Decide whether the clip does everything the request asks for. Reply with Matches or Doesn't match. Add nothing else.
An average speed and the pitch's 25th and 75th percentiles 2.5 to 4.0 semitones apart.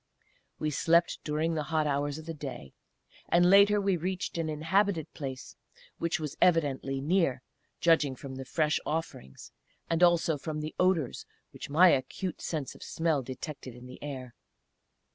Matches